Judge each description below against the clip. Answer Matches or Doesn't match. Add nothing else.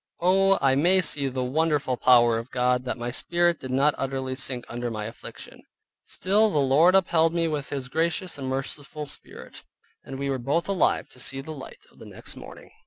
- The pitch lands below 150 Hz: Matches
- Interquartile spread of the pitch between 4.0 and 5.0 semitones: Matches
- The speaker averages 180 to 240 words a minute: Matches